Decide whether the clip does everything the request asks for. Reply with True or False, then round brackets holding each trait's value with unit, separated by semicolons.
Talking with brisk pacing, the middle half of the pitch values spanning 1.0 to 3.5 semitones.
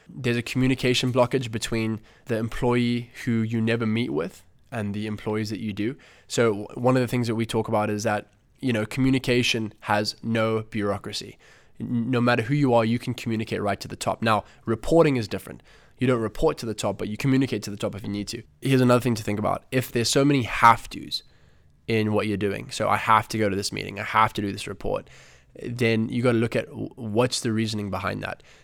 True (225 wpm; 2.6 semitones)